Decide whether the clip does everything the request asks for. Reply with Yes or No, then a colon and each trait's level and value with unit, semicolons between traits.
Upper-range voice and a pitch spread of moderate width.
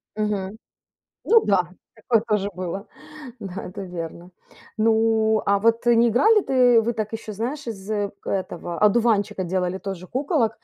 Yes: high, 215 Hz; average, 3.3 semitones